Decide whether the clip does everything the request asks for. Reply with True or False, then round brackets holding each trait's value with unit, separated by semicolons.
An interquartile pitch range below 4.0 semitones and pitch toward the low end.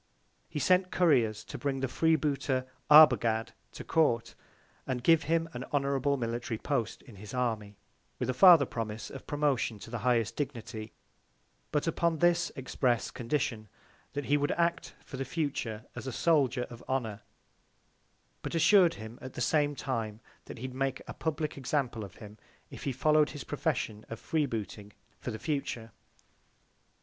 False (4.5 semitones; 130 Hz)